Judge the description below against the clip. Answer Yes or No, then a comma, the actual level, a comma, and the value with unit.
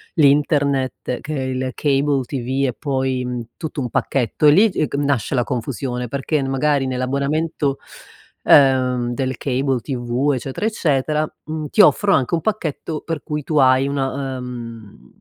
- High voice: No, low, 135 Hz